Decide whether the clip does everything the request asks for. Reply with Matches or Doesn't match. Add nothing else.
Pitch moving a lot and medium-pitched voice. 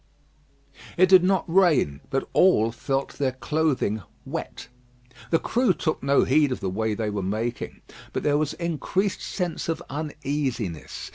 Matches